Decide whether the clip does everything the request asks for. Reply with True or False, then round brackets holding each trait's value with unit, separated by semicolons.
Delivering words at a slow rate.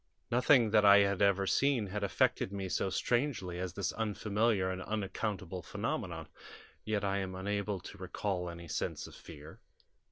False (160 wpm)